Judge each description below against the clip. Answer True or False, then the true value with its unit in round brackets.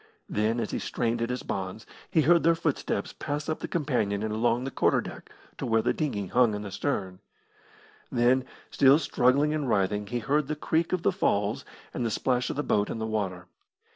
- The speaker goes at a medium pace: False (210 wpm)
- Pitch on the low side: True (120 Hz)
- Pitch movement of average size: False (5.7 semitones)